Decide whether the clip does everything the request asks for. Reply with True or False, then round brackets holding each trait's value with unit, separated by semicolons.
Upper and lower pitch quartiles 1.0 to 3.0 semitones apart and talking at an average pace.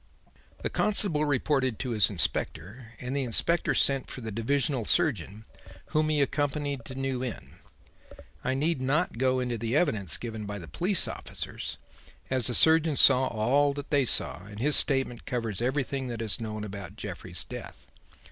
False (4.1 semitones; 165 wpm)